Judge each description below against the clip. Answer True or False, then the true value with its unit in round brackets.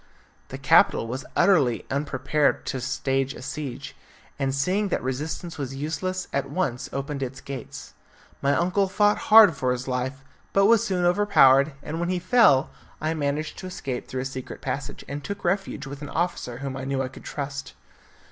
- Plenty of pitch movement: False (4.9 semitones)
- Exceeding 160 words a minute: True (180 wpm)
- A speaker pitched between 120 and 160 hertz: True (140 Hz)